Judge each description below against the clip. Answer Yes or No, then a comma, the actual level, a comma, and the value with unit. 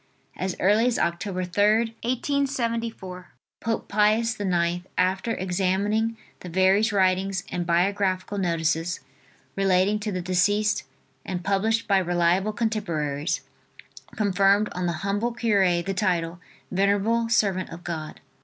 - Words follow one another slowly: Yes, slow, 120 wpm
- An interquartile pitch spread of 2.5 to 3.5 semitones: Yes, average, 3.1 semitones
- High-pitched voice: Yes, high, 195 Hz